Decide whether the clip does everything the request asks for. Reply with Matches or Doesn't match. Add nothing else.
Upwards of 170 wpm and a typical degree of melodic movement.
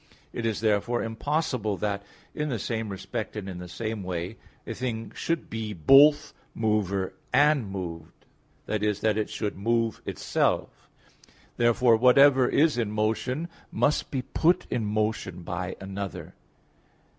Doesn't match